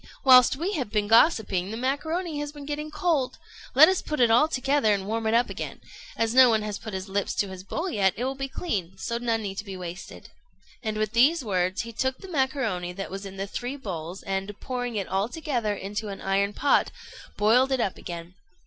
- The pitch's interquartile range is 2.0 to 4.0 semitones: No, wide, 5.4 semitones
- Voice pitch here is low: No, high, 225 Hz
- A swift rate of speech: Yes, fast, 220 wpm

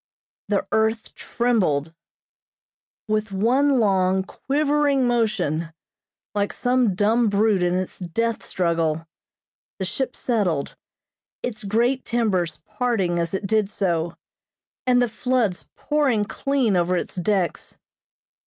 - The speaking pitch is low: No, high, 210 Hz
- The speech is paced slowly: Yes, slow, 115 wpm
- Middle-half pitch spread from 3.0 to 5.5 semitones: Yes, average, 5.0 semitones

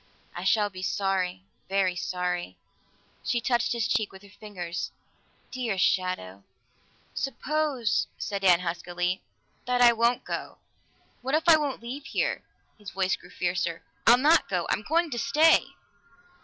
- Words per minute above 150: No, average, 145 wpm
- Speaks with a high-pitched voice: Yes, high, 200 Hz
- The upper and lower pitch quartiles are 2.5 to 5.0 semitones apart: No, wide, 5.4 semitones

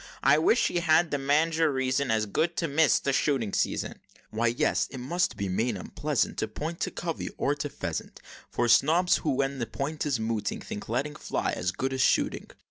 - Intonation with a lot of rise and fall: No, average, 5.0 semitones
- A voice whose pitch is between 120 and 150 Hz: Yes, medium, 140 Hz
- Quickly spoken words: Yes, fast, 210 wpm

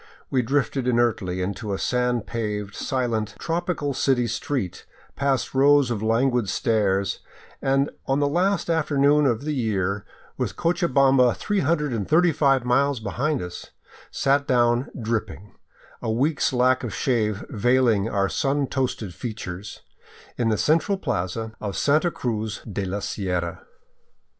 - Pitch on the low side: Yes, low, 125 Hz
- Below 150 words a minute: Yes, slow, 135 wpm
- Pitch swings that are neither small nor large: Yes, average, 4.8 semitones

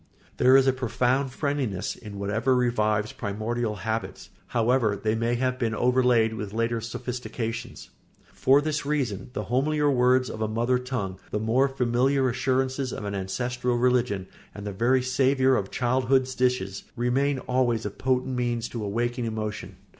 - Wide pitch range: No, average, 2.8 semitones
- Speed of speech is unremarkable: Yes, average, 155 wpm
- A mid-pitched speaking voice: No, low, 125 Hz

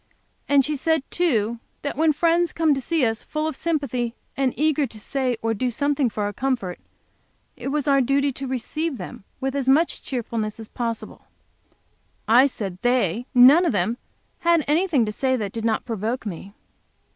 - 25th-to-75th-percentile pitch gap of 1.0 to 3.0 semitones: No, average, 4.4 semitones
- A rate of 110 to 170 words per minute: No, average, 180 wpm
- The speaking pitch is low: No, very high, 260 Hz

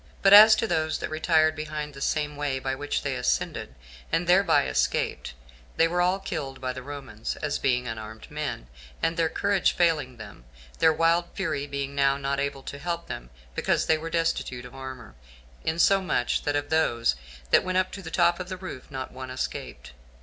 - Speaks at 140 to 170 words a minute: No, average, 195 wpm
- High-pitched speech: No, medium, 150 Hz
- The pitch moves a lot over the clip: No, average, 4.2 semitones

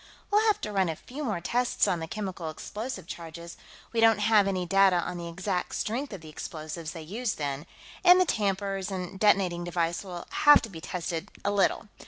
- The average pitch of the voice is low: No, high, 190 Hz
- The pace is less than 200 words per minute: No, fast, 205 wpm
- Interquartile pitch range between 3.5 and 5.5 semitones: Yes, average, 3.9 semitones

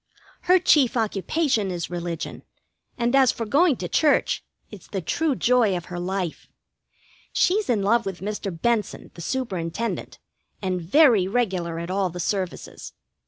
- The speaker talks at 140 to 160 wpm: Yes, average, 150 wpm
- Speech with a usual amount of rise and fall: No, wide, 5.7 semitones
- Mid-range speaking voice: No, high, 205 Hz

